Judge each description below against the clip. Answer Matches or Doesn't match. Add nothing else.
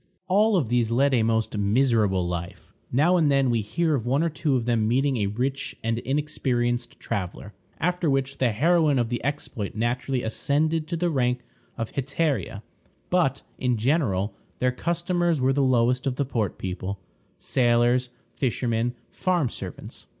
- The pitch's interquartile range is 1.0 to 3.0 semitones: Doesn't match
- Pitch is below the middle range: Matches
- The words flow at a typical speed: Matches